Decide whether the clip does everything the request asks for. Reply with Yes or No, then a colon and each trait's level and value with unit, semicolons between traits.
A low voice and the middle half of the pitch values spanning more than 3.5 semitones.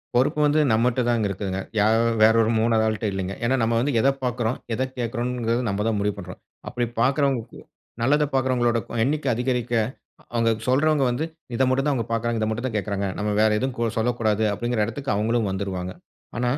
No: low, 115 Hz; average, 2.7 semitones